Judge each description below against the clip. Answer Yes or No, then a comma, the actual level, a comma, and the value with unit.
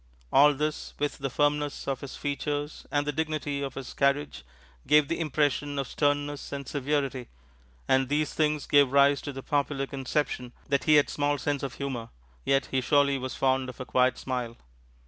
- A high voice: No, medium, 140 Hz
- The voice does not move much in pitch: Yes, narrow, 1.6 semitones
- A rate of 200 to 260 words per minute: No, average, 185 wpm